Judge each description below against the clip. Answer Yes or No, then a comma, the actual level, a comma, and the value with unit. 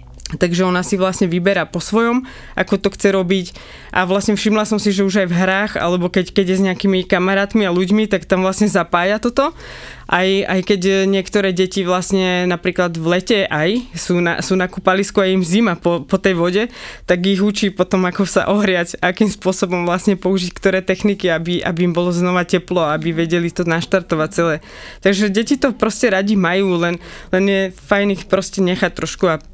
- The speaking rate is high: Yes, fast, 195 wpm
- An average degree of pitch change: No, narrow, 2.1 semitones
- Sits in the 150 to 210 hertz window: Yes, high, 190 Hz